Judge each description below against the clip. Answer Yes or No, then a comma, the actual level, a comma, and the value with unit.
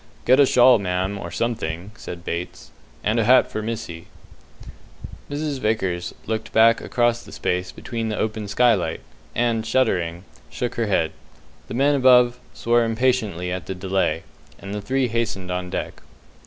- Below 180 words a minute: Yes, average, 155 wpm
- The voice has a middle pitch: No, low, 110 Hz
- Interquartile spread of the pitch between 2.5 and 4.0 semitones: No, average, 4.8 semitones